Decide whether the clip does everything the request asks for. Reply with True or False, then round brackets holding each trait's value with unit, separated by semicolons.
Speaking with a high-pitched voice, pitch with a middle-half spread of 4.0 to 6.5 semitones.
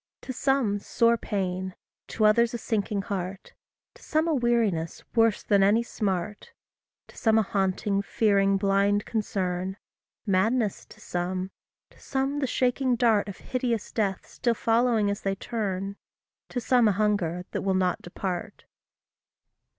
False (205 Hz; 3.3 semitones)